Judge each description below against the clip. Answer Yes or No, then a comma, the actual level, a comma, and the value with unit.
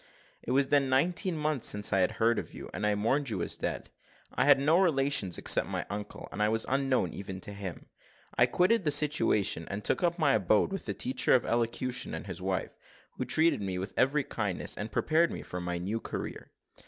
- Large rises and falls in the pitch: Yes, wide, 6.1 semitones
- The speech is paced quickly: Yes, fast, 215 wpm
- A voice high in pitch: No, low, 125 Hz